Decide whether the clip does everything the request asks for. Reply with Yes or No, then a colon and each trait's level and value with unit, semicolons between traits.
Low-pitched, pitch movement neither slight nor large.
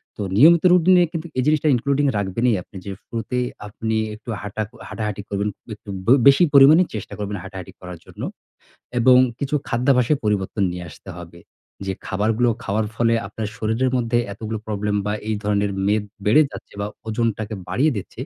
Yes: low, 110 Hz; average, 3.7 semitones